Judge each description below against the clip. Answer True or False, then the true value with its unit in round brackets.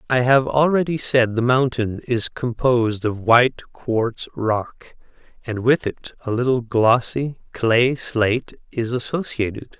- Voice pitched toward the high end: False (120 Hz)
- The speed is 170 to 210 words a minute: False (135 wpm)